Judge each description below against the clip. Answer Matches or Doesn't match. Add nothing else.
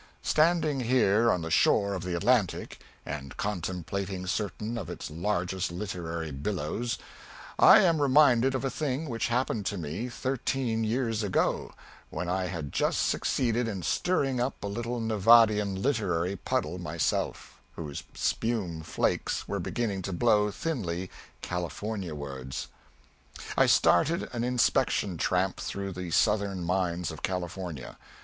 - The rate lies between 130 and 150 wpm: Matches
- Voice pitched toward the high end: Doesn't match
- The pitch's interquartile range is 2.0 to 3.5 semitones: Doesn't match